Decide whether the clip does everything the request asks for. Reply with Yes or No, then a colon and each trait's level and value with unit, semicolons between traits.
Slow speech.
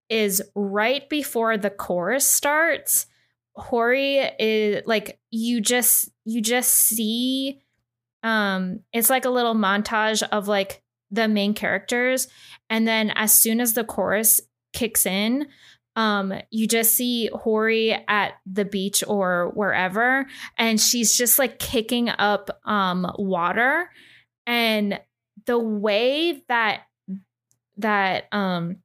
Yes: slow, 120 wpm